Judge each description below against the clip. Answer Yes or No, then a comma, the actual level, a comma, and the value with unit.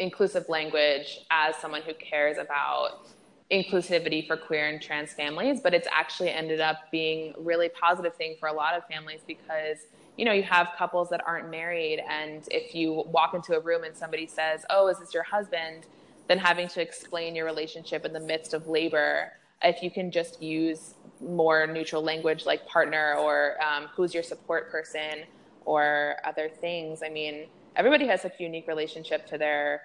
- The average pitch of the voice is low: No, medium, 160 Hz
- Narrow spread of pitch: Yes, narrow, 1.8 semitones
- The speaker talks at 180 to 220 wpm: Yes, average, 185 wpm